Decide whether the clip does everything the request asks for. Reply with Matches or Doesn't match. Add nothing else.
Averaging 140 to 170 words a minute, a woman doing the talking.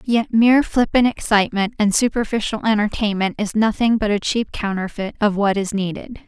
Matches